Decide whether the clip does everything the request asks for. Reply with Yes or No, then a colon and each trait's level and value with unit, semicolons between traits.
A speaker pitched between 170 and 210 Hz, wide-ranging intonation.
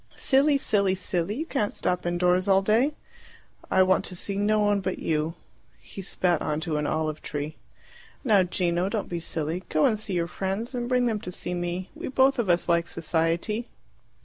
No: medium, 185 Hz; average, 3.9 semitones